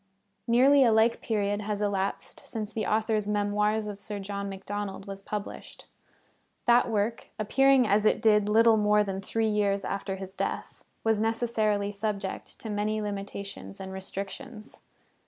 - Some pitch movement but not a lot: No, narrow, 1.7 semitones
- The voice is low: No, high, 210 Hz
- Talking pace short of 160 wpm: Yes, average, 150 wpm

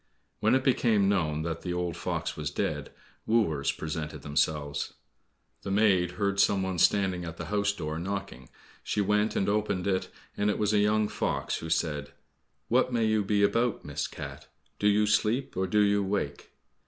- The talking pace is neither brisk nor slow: Yes, average, 180 wpm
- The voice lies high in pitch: No, low, 100 Hz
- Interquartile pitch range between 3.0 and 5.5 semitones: Yes, average, 4.3 semitones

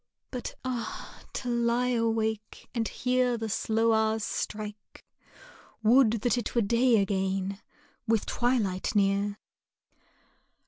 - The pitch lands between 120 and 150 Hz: No, high, 225 Hz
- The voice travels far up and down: No, narrow, 2.6 semitones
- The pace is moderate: No, slow, 110 wpm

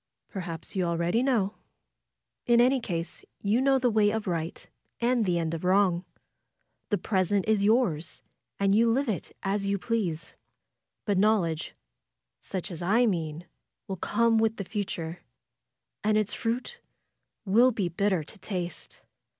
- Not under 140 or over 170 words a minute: Yes, average, 150 wpm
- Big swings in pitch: No, average, 4.5 semitones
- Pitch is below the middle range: No, high, 200 Hz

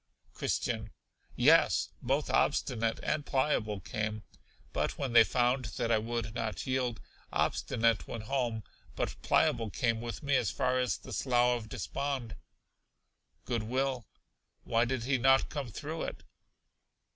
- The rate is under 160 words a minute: Yes, average, 140 wpm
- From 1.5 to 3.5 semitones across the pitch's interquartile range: Yes, narrow, 2.6 semitones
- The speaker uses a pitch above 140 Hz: No, low, 120 Hz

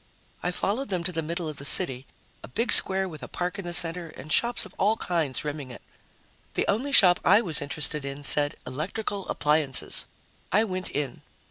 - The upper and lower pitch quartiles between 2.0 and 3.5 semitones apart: No, average, 4.7 semitones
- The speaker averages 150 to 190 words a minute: No, average, 200 wpm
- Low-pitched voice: No, medium, 170 Hz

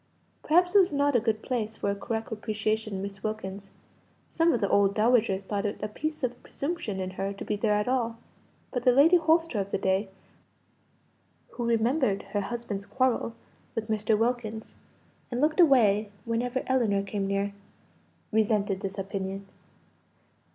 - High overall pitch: Yes, high, 220 Hz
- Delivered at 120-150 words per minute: No, average, 165 wpm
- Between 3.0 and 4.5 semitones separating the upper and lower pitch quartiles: Yes, average, 3.7 semitones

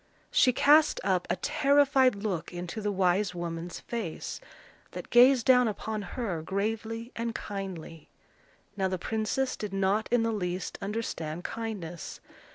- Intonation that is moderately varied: Yes, average, 4.4 semitones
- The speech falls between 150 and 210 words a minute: No, average, 140 wpm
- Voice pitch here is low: No, high, 205 Hz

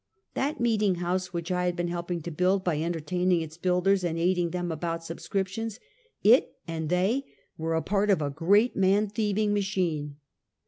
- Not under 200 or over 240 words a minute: No, average, 175 wpm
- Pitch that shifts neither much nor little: Yes, average, 3.0 semitones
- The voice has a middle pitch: Yes, medium, 180 Hz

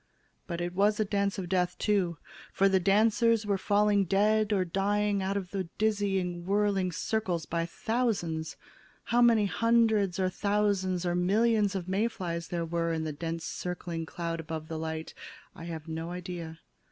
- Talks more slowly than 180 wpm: Yes, average, 170 wpm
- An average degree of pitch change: Yes, average, 3.4 semitones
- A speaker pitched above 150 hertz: Yes, high, 190 Hz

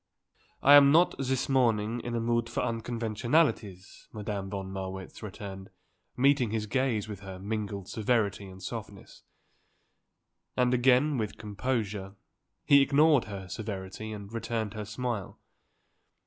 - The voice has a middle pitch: No, low, 110 Hz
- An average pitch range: Yes, average, 3.8 semitones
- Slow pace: Yes, slow, 130 wpm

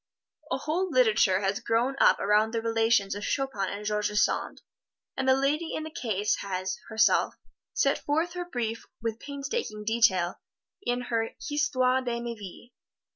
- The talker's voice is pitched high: Yes, high, 230 Hz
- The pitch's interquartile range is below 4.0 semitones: No, average, 4.5 semitones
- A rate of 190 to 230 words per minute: No, average, 160 wpm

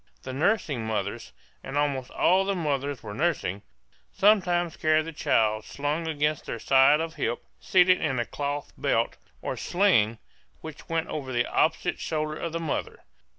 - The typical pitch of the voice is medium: Yes, medium, 150 Hz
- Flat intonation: No, average, 4.1 semitones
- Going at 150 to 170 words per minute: Yes, average, 160 wpm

